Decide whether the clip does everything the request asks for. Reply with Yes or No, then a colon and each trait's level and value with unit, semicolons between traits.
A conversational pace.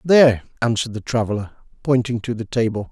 Yes: average, 165 wpm